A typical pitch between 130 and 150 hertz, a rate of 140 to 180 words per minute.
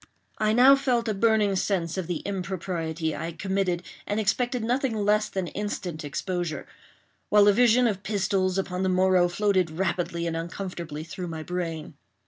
No: high, 190 Hz; average, 165 wpm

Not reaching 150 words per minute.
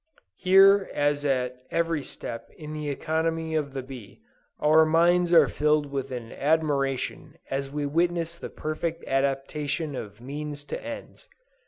Yes: average, 140 wpm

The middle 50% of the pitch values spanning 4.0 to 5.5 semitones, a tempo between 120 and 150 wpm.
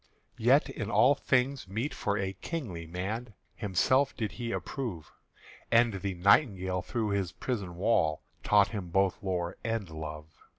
Yes: average, 4.5 semitones; average, 145 wpm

